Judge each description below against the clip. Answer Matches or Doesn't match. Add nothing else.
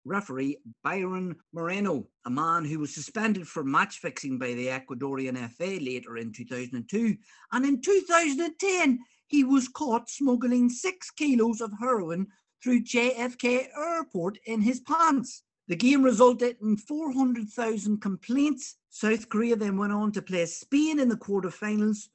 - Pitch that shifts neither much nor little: Doesn't match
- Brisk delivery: Doesn't match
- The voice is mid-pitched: Doesn't match